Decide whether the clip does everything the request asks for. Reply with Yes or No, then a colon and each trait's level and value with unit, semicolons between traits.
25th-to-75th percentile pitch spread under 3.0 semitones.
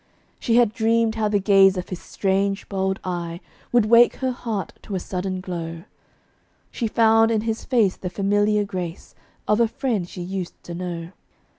No: average, 3.5 semitones